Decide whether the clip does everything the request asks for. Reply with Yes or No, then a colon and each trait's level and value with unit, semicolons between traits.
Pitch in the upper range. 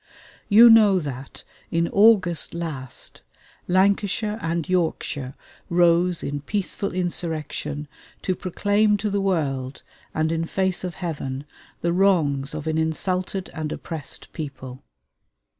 No: medium, 170 Hz